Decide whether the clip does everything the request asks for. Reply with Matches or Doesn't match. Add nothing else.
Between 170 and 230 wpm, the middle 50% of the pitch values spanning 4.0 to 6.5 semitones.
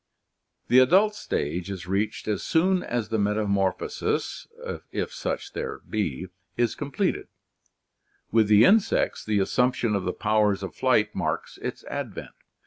Doesn't match